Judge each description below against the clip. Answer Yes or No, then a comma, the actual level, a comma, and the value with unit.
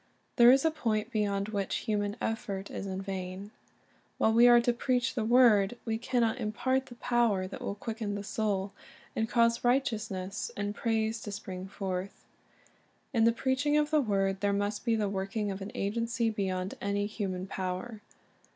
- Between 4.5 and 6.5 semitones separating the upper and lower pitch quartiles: No, average, 3.1 semitones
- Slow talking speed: No, average, 185 wpm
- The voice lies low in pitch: No, high, 215 Hz